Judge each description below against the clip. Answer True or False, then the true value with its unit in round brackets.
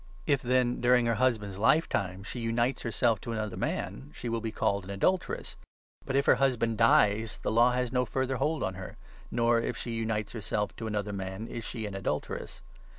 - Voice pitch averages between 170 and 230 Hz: False (115 Hz)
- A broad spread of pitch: False (3.0 semitones)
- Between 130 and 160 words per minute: False (205 wpm)